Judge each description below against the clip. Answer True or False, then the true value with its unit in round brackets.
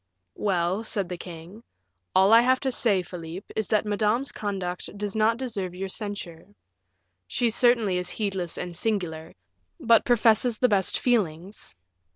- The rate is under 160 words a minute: True (150 wpm)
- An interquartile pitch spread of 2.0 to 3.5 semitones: False (3.9 semitones)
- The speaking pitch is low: False (205 Hz)